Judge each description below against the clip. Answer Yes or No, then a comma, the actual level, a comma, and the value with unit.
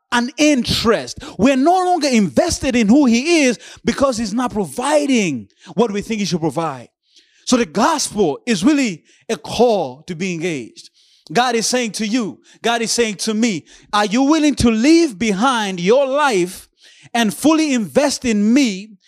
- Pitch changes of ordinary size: Yes, average, 4.9 semitones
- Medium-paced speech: Yes, average, 165 wpm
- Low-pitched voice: No, high, 235 Hz